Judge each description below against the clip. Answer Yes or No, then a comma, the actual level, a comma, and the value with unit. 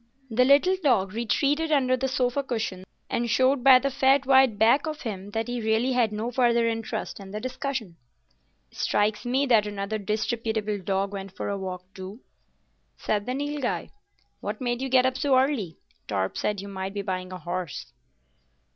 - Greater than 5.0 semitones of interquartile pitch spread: No, average, 4.6 semitones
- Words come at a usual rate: Yes, average, 180 wpm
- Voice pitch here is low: No, high, 230 Hz